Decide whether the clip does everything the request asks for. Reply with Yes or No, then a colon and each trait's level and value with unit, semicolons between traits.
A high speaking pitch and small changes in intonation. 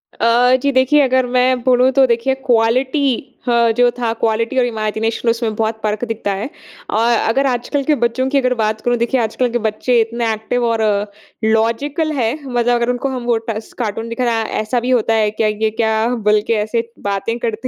Yes: high, 235 Hz; narrow, 2.3 semitones